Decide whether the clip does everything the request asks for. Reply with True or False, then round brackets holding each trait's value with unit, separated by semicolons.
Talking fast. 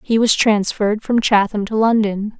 False (175 wpm)